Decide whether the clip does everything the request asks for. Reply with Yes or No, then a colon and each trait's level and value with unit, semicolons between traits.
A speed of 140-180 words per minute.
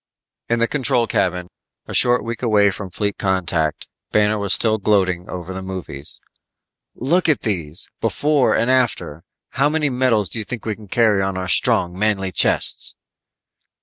Yes: average, 160 wpm